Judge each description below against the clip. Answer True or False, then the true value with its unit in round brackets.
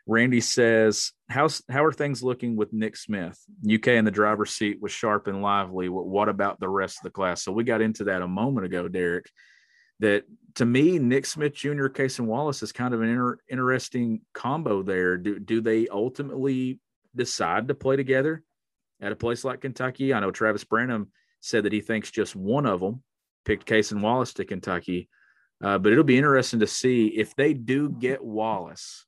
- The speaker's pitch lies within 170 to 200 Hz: False (115 Hz)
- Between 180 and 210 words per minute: True (200 wpm)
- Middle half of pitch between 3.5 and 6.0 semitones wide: True (3.8 semitones)